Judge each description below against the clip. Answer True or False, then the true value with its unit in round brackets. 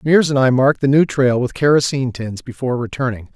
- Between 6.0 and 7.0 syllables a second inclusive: True (6.4 syllables/s)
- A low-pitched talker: True (130 Hz)